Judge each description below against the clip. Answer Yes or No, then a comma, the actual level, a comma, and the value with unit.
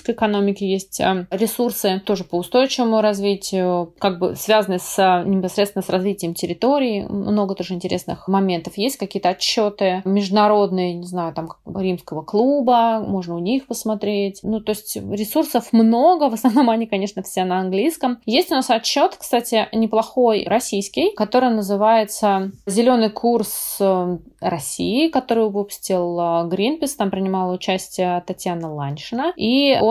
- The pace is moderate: Yes, average, 135 wpm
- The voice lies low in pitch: No, high, 205 Hz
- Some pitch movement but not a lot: Yes, average, 3.6 semitones